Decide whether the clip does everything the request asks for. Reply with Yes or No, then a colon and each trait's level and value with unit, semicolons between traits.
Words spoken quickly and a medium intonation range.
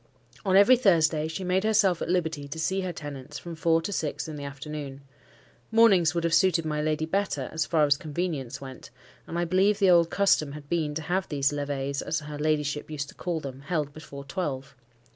Yes: fast, 210 wpm; average, 3.6 semitones